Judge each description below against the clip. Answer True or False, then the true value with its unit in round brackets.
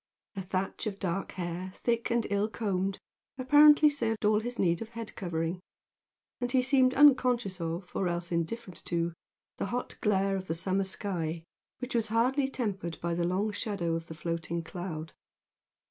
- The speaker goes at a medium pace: True (170 wpm)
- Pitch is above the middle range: True (195 Hz)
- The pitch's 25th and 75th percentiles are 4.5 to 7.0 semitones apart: True (5.3 semitones)